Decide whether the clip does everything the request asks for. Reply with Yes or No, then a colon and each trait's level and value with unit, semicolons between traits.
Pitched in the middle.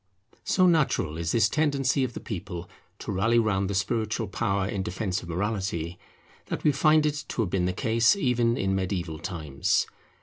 No: low, 100 Hz